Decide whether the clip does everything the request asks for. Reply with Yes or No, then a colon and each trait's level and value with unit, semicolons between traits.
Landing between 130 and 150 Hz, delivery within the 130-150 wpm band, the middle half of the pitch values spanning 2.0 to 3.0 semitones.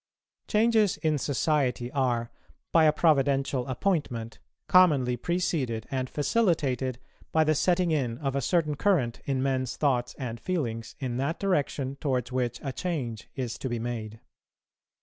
No: low, 135 Hz; average, 145 wpm; average, 4.4 semitones